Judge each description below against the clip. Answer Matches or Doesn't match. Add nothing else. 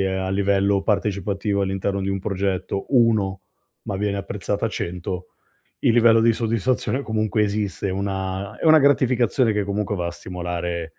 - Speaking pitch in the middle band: Doesn't match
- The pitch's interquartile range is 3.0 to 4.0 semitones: Doesn't match